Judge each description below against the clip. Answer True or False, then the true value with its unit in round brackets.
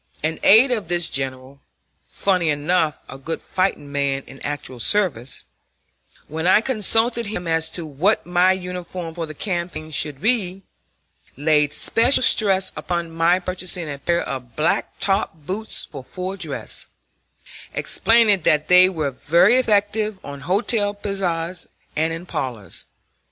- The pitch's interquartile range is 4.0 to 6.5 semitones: True (4.5 semitones)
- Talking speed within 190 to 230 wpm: False (140 wpm)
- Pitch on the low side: False (175 Hz)